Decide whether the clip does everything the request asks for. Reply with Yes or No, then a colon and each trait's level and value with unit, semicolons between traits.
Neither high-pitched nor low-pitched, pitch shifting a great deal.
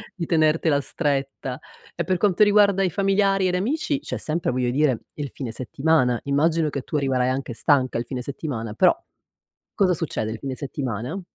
Yes: medium, 145 Hz; wide, 5.9 semitones